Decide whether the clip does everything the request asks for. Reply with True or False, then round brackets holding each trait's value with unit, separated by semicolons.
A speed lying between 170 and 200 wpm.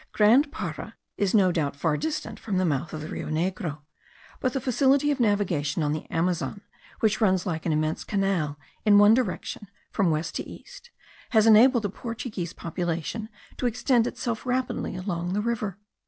True (175 wpm)